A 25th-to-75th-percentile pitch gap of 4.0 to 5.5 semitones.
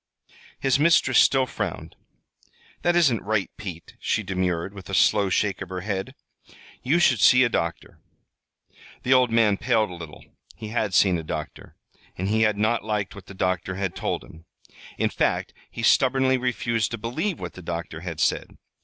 Yes: average, 4.9 semitones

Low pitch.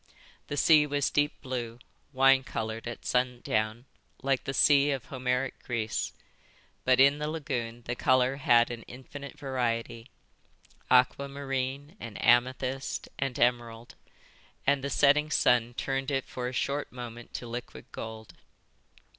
Yes: low, 130 Hz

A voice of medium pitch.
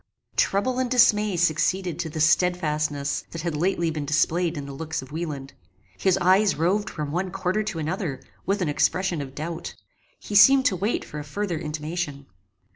Yes: medium, 170 Hz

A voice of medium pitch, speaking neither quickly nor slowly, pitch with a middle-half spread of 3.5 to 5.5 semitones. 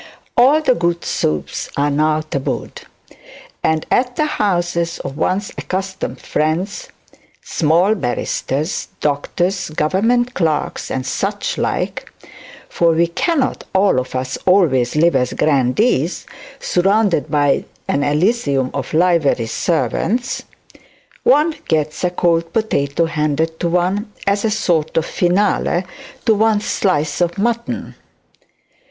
No: medium, 170 Hz; slow, 120 wpm; average, 5.1 semitones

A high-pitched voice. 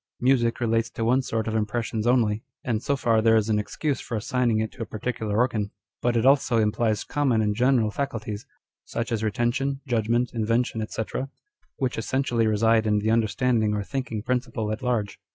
No: low, 115 Hz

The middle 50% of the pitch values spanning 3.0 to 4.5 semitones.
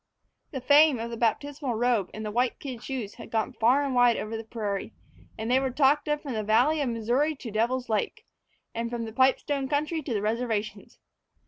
Yes: average, 3.5 semitones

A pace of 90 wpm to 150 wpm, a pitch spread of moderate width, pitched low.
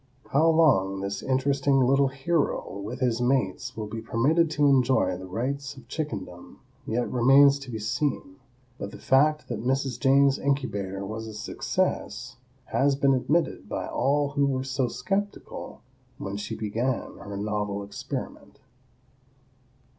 Yes: average, 145 wpm; average, 4.6 semitones; low, 130 Hz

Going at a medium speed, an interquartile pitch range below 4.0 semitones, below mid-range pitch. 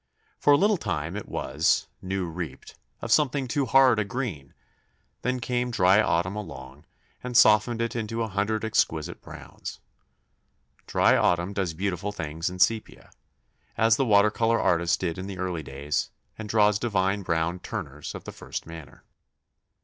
No: average, 160 wpm; average, 5.2 semitones; low, 100 Hz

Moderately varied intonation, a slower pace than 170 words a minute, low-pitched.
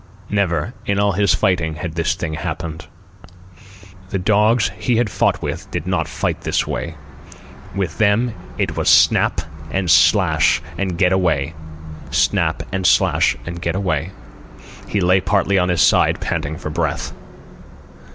Yes: average, 3.5 semitones; average, 150 wpm; very low, 90 Hz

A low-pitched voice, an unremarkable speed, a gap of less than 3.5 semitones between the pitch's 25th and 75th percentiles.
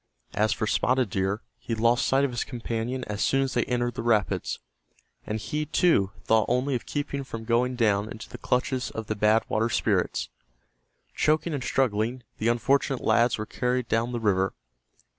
Yes: low, 120 Hz; average, 185 wpm; average, 2.9 semitones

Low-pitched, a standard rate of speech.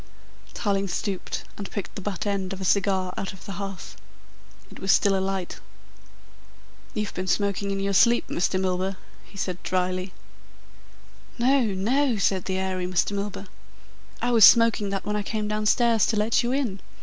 No: high, 200 Hz; average, 170 wpm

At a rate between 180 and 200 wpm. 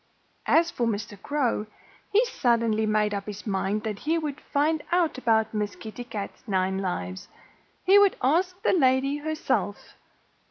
No: average, 155 wpm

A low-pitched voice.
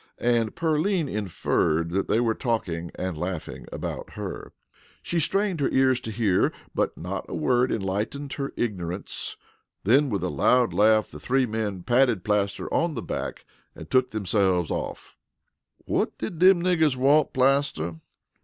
Yes: low, 115 Hz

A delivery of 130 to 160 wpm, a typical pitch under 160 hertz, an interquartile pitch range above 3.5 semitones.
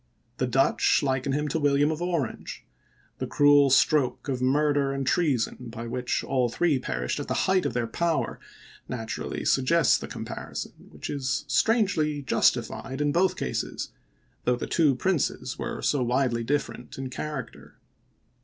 No: average, 155 wpm; low, 135 Hz; average, 3.2 semitones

